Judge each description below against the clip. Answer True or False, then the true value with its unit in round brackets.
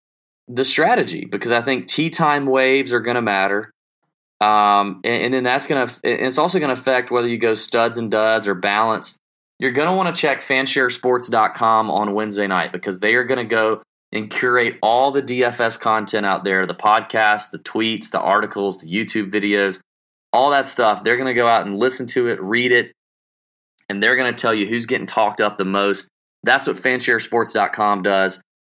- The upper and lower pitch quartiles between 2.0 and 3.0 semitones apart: False (3.4 semitones)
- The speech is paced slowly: False (195 wpm)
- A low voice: True (115 Hz)